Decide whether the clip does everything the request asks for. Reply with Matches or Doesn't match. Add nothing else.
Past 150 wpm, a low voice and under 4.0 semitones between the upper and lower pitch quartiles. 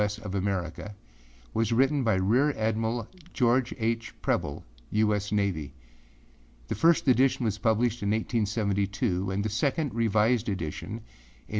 Doesn't match